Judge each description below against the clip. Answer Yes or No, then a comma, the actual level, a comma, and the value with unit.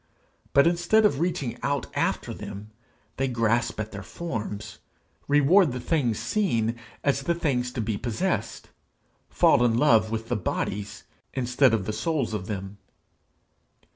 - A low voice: Yes, low, 120 Hz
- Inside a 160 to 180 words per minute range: No, average, 145 wpm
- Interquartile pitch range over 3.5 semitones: Yes, average, 5.1 semitones